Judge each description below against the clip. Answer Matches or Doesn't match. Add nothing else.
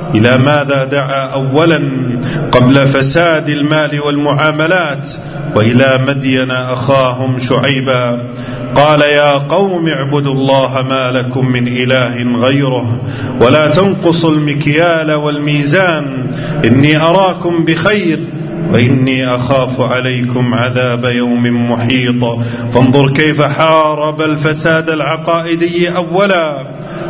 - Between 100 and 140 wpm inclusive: Doesn't match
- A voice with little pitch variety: Doesn't match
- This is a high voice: Doesn't match